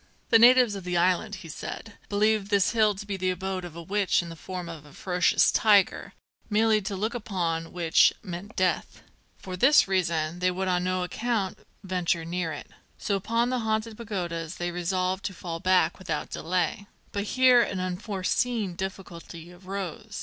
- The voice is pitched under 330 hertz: Yes, medium, 185 Hz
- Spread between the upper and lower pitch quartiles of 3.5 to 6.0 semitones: No, average, 3.0 semitones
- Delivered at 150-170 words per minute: No, average, 180 wpm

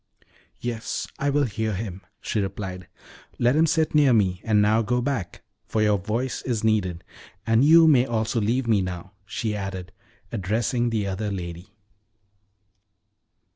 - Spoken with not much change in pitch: No, average, 3.8 semitones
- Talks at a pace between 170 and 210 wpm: No, average, 150 wpm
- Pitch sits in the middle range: No, low, 110 Hz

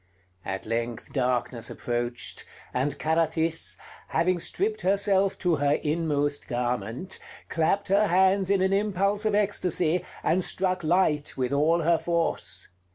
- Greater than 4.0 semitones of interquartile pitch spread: Yes, average, 5.1 semitones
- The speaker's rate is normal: No, slow, 130 wpm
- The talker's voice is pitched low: No, medium, 165 Hz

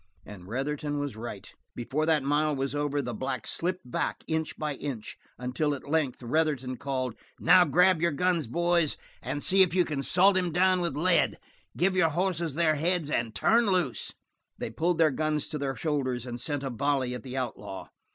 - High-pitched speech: No, medium, 150 Hz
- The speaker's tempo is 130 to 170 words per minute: No, average, 190 wpm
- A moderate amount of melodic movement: Yes, average, 4.6 semitones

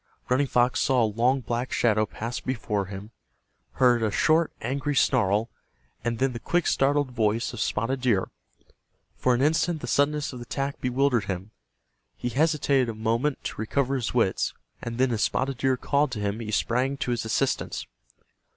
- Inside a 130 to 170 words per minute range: No, average, 180 wpm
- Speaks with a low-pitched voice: Yes, low, 125 Hz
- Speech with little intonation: No, average, 3.4 semitones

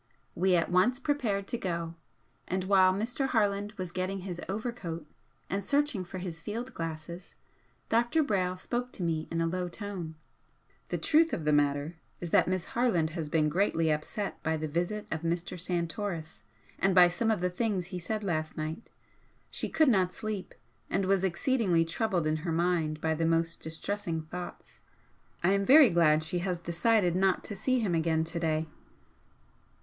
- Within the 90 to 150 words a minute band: No, average, 175 wpm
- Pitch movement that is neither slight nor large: Yes, average, 3.7 semitones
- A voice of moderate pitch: Yes, medium, 180 Hz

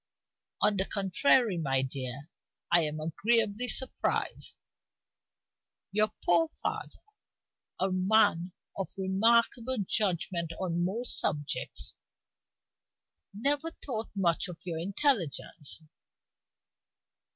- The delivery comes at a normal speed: No, slow, 90 wpm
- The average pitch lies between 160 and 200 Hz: Yes, high, 190 Hz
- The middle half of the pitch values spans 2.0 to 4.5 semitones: No, average, 4.9 semitones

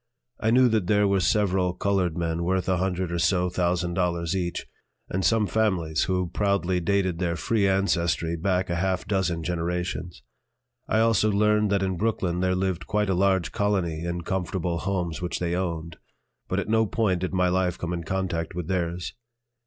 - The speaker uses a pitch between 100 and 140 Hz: No, very low, 90 Hz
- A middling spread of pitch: No, narrow, 2.1 semitones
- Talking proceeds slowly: No, average, 185 wpm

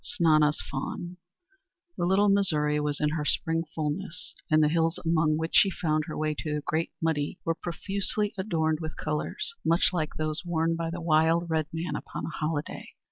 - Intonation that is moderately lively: No, narrow, 1.9 semitones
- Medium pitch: Yes, medium, 160 Hz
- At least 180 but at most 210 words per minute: Yes, average, 190 wpm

